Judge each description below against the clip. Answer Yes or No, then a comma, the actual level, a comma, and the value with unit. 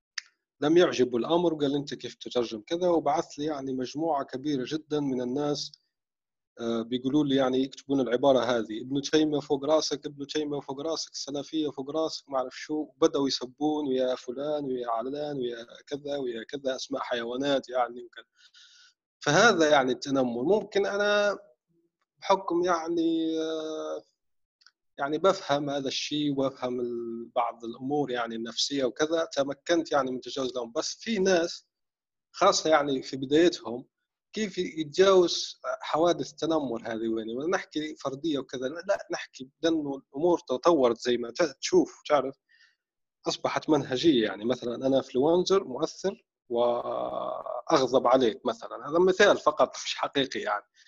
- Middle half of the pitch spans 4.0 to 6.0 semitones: Yes, average, 4.5 semitones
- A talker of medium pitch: Yes, medium, 145 Hz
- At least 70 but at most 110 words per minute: No, average, 130 wpm